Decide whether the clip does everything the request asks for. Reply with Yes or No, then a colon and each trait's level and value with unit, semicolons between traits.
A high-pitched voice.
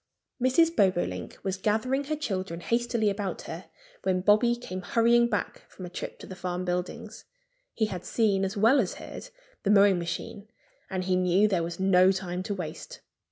Yes: high, 195 Hz